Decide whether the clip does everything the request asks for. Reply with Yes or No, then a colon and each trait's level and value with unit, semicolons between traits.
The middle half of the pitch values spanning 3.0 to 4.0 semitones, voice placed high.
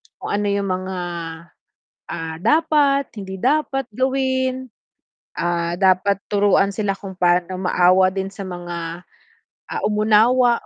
No: wide, 5.5 semitones; high, 200 Hz